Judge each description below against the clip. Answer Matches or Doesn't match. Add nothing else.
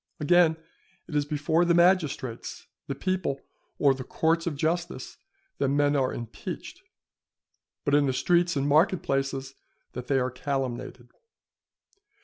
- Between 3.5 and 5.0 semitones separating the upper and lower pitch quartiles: Matches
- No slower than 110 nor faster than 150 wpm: Matches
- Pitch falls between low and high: Matches